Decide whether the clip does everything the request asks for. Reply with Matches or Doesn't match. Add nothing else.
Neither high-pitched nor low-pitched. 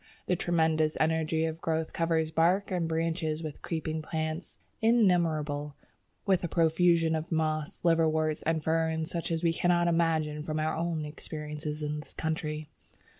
Matches